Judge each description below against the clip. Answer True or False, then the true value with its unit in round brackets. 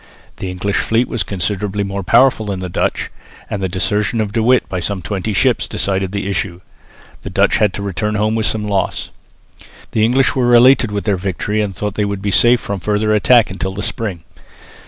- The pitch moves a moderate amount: False (2.2 semitones)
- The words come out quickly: True (210 wpm)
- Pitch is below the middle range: True (105 Hz)